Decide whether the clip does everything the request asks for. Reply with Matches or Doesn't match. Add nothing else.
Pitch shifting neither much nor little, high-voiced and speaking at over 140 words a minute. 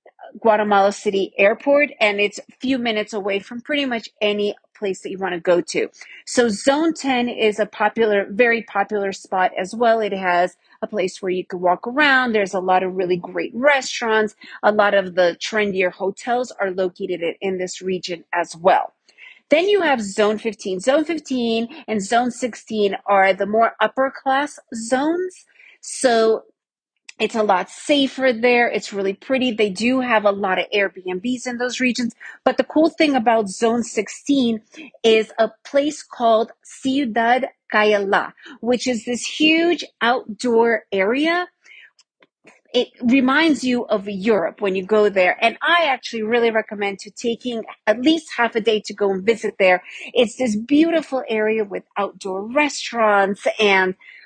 Matches